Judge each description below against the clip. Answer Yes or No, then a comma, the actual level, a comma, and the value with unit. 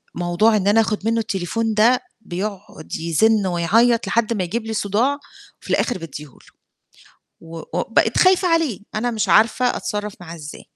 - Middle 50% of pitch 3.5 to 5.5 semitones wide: Yes, average, 4.5 semitones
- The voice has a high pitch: Yes, high, 215 Hz